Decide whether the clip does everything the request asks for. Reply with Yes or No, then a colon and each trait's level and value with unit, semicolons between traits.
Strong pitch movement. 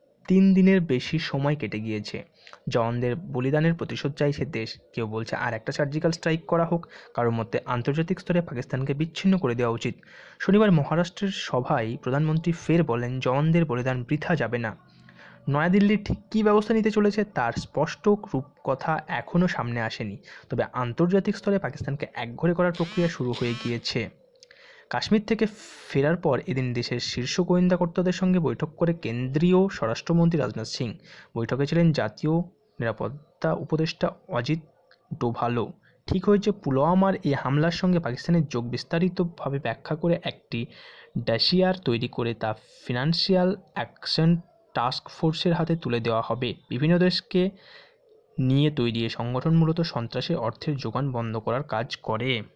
Yes: wide, 6.4 semitones